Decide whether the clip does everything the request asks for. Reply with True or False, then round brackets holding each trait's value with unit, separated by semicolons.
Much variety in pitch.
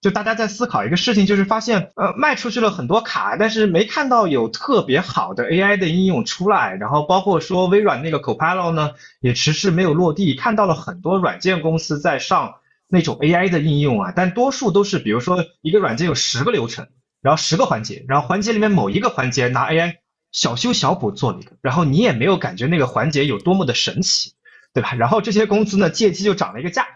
False (4.8 semitones)